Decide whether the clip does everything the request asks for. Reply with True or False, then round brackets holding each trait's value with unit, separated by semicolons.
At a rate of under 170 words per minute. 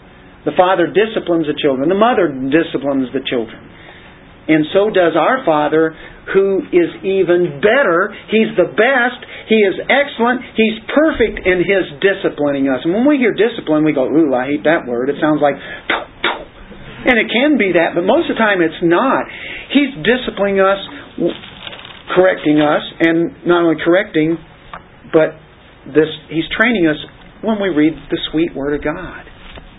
True (160 wpm)